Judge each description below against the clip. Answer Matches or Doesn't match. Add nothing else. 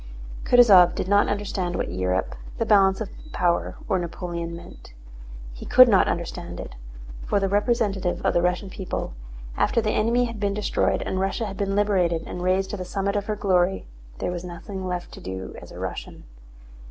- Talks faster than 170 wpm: Matches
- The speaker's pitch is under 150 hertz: Doesn't match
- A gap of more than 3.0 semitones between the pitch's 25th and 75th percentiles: Doesn't match